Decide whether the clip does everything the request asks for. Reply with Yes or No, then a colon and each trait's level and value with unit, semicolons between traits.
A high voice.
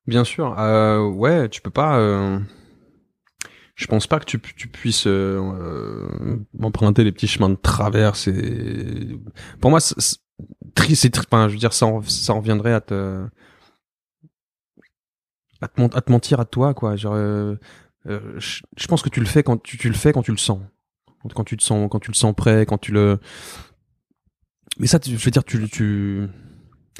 No: low, 110 Hz